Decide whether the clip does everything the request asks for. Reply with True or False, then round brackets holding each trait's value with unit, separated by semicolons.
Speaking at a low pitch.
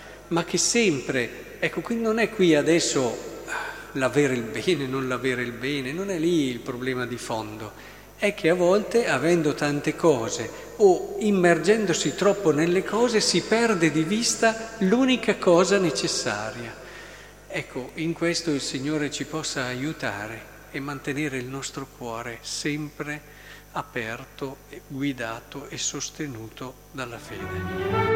False (155 Hz)